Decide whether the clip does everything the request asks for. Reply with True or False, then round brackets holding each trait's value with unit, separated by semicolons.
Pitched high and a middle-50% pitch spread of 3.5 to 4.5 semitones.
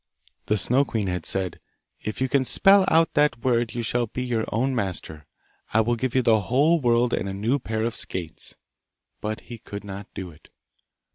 False (115 Hz; 4.1 semitones)